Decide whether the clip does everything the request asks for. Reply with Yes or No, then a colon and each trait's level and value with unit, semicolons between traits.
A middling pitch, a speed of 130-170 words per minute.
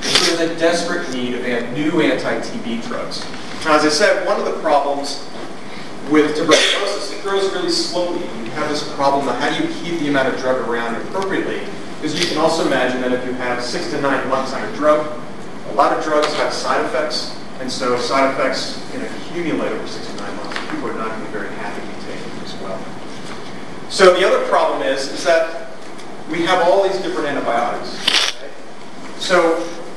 No: medium, 150 Hz; fast, 205 wpm